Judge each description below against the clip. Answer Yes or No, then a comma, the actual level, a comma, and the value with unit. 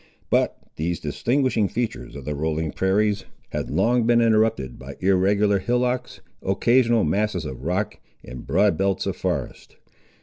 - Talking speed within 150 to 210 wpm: No, average, 140 wpm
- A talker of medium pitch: No, low, 100 Hz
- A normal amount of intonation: No, wide, 6.2 semitones